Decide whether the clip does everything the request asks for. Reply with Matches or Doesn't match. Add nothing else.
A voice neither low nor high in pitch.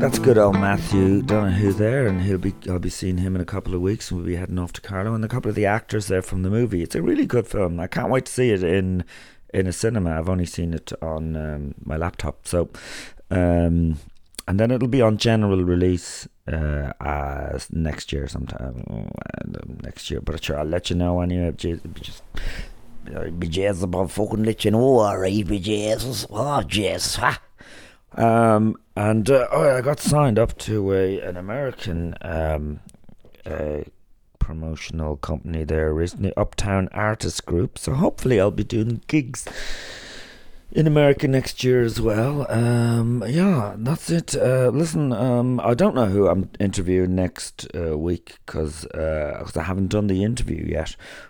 Doesn't match